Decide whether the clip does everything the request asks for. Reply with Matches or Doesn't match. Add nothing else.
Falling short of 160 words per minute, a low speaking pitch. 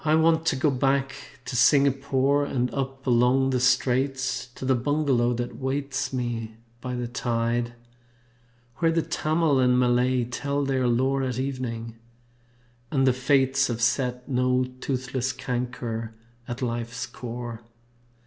Matches